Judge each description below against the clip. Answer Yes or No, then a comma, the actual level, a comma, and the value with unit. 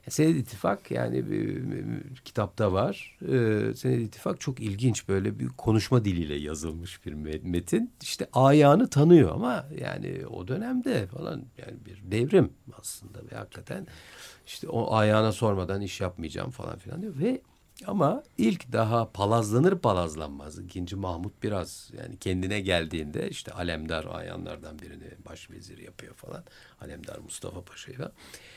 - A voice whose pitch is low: Yes, low, 105 Hz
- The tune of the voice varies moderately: No, wide, 6.1 semitones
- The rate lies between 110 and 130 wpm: No, fast, 140 wpm